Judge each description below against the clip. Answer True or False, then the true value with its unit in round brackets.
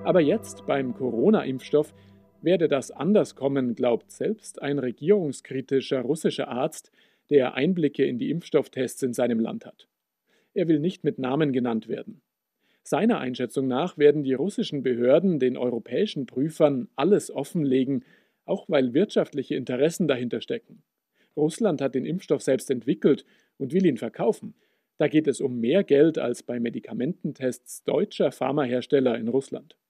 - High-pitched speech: False (135 Hz)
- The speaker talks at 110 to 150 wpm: True (145 wpm)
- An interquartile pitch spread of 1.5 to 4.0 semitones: True (3.4 semitones)